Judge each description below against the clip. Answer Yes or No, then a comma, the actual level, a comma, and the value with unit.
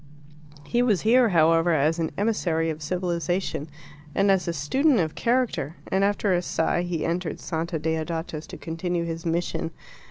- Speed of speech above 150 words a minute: Yes, average, 160 wpm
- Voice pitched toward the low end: No, medium, 170 Hz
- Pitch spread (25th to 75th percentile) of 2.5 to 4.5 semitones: Yes, average, 3.0 semitones